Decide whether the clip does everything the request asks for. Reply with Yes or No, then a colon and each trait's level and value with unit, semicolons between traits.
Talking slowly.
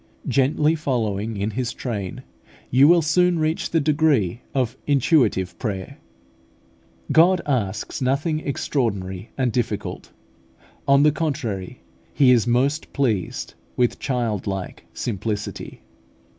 Yes: slow, 110 wpm